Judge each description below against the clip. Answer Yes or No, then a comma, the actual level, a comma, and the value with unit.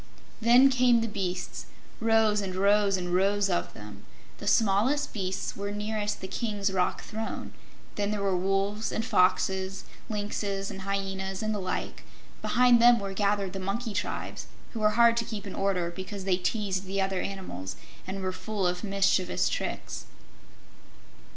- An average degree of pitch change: No, narrow, 2.2 semitones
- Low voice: No, high, 200 Hz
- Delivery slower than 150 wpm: No, average, 165 wpm